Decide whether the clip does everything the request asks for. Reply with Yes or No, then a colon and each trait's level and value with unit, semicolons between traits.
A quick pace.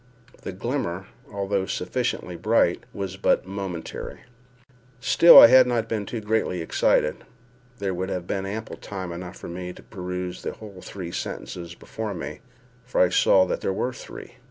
No: average, 155 wpm